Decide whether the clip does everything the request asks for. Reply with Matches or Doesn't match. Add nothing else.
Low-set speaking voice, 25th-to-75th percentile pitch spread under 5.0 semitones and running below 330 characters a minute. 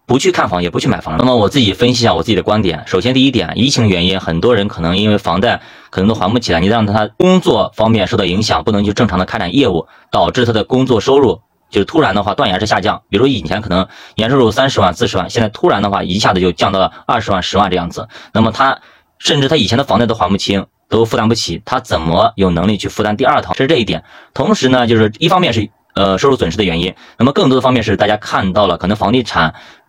Doesn't match